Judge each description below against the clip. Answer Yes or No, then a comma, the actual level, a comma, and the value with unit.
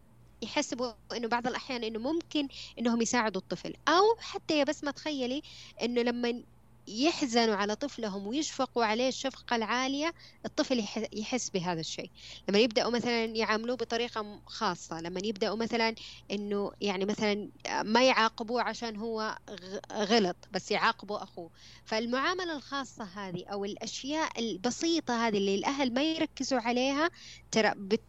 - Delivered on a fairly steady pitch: No, average, 3.9 semitones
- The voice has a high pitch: Yes, high, 235 Hz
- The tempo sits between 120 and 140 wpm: Yes, average, 130 wpm